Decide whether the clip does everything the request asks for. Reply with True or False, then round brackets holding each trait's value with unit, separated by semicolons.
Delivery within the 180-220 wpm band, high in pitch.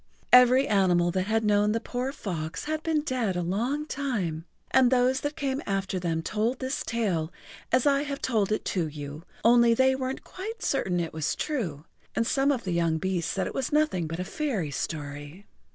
True (200 wpm; 220 Hz)